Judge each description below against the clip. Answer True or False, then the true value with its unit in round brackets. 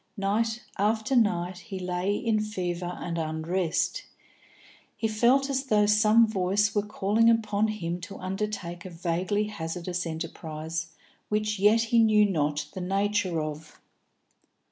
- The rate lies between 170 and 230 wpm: False (135 wpm)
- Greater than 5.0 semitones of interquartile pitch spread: False (3.5 semitones)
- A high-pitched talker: True (200 Hz)